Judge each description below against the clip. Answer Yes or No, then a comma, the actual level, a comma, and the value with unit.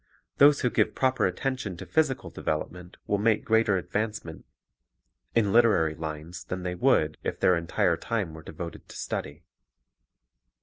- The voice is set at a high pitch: No, very low, 95 Hz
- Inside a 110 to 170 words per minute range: Yes, average, 160 wpm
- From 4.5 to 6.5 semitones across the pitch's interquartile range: Yes, average, 5.2 semitones